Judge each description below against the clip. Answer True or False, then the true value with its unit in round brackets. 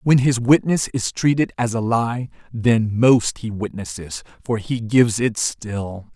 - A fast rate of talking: False (165 wpm)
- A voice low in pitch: True (115 Hz)